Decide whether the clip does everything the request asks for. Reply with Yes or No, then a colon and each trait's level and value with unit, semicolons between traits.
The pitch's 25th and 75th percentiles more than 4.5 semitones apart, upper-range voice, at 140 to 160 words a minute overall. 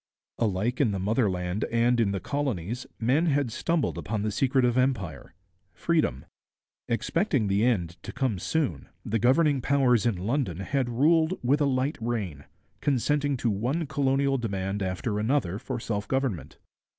No: wide, 5.6 semitones; low, 120 Hz; average, 155 wpm